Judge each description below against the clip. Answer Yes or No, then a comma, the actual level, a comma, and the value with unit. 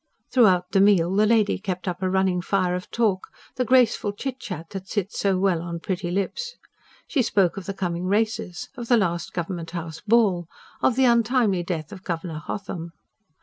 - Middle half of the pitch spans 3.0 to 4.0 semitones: Yes, average, 3.7 semitones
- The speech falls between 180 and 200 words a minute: Yes, average, 185 wpm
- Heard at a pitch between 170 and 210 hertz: Yes, high, 190 Hz